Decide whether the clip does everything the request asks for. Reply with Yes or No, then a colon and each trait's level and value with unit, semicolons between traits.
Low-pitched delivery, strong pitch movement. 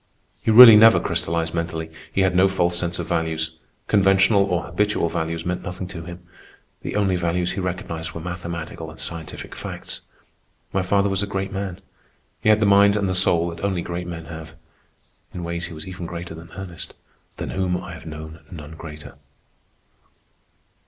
No: very low, 85 Hz; narrow, 2.5 semitones